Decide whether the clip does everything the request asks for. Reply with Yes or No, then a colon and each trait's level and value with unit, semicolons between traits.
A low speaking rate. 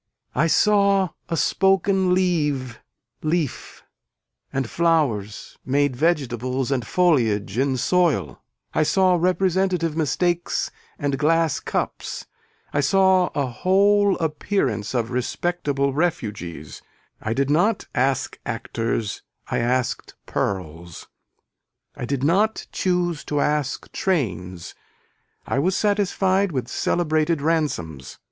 Yes: slow, 105 wpm